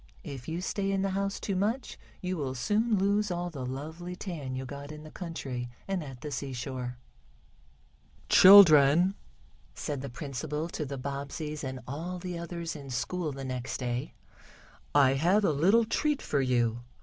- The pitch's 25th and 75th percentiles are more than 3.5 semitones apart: Yes, average, 5.3 semitones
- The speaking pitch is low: No, medium, 150 Hz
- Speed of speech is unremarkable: Yes, average, 170 wpm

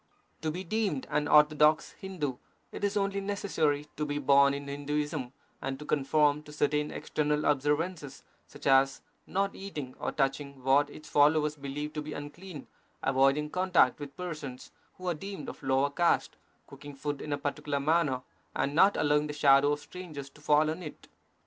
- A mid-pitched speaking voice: Yes, medium, 150 Hz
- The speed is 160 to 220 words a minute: Yes, average, 175 wpm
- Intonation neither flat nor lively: No, narrow, 1.9 semitones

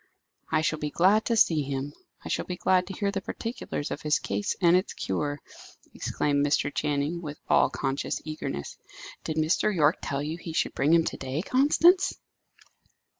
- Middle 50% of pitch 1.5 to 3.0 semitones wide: No, average, 4.3 semitones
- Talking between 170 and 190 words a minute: Yes, average, 180 wpm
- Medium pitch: Yes, medium, 155 Hz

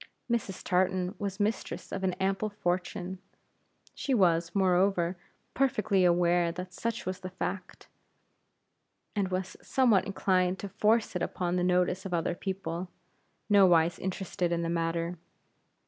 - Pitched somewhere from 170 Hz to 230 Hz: Yes, medium, 185 Hz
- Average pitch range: No, narrow, 1.8 semitones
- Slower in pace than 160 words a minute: Yes, slow, 135 wpm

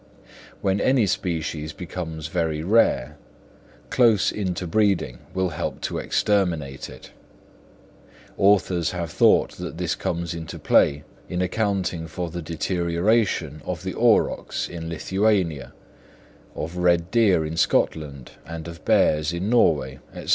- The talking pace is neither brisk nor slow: No, slow, 125 wpm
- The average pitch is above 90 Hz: No, very low, 85 Hz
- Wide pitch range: No, average, 3.2 semitones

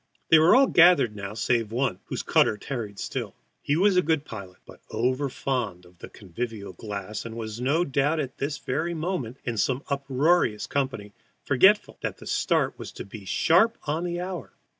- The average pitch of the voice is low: Yes, low, 130 Hz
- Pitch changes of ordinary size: No, wide, 6.9 semitones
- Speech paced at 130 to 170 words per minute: No, average, 180 wpm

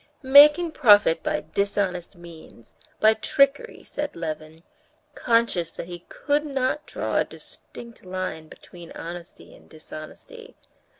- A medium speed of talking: No, slow, 120 wpm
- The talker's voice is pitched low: No, high, 200 Hz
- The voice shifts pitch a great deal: Yes, wide, 8.6 semitones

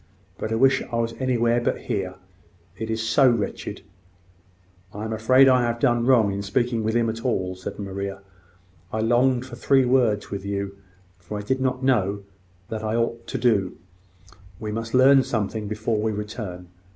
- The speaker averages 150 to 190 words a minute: Yes, average, 180 wpm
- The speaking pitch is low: Yes, low, 115 Hz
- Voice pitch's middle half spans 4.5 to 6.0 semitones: No, average, 3.0 semitones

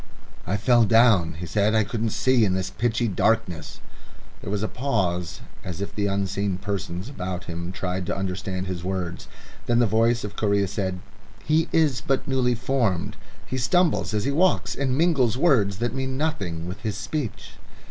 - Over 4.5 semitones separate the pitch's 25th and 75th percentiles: Yes, average, 4.9 semitones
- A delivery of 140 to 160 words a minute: No, average, 180 wpm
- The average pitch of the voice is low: Yes, low, 105 Hz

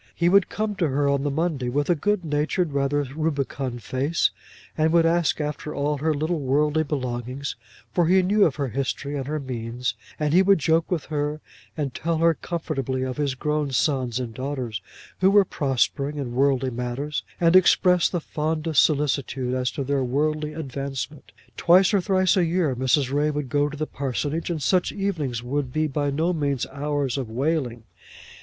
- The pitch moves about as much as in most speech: Yes, average, 3.3 semitones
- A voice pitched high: No, medium, 145 Hz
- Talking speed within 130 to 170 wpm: No, average, 185 wpm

